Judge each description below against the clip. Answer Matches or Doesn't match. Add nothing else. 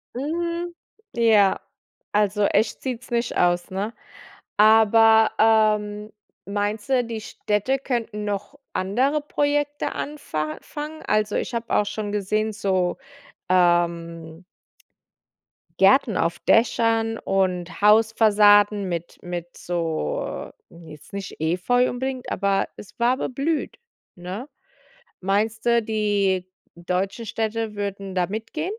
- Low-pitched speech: Doesn't match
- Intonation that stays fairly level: Doesn't match